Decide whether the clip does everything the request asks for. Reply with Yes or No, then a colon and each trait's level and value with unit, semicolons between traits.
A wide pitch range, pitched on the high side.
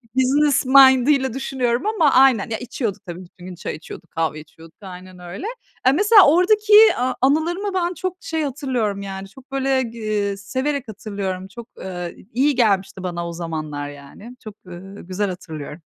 Yes: wide, 6.7 semitones; high, 225 Hz